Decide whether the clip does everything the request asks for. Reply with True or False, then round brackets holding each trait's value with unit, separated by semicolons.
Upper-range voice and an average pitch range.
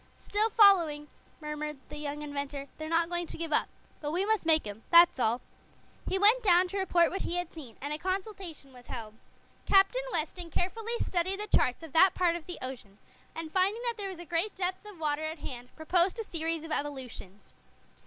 True (330 Hz; 4.3 semitones)